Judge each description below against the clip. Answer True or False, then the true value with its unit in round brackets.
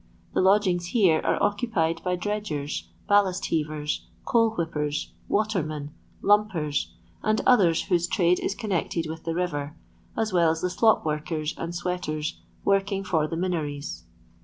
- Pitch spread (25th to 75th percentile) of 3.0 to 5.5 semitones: True (4.3 semitones)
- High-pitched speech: False (175 Hz)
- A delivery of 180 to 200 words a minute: False (145 wpm)